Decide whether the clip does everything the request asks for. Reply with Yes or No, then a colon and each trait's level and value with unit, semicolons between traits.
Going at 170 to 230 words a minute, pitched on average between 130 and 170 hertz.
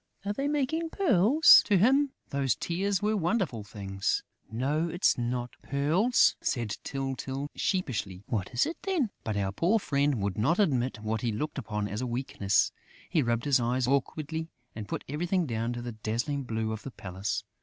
Yes: average, 175 wpm; low, 135 Hz